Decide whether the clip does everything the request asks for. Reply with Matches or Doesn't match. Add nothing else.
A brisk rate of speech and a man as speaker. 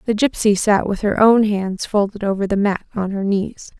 Doesn't match